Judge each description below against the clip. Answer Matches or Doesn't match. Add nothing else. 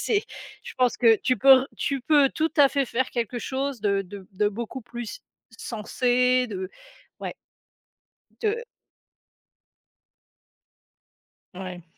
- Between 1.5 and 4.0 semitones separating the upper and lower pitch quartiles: Doesn't match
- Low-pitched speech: Doesn't match